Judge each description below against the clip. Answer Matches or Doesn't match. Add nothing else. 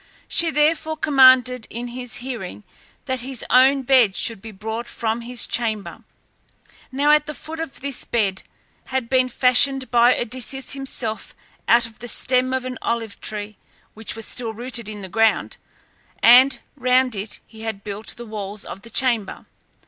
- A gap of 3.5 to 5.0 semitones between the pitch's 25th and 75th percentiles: Doesn't match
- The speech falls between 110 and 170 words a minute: Matches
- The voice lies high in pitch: Matches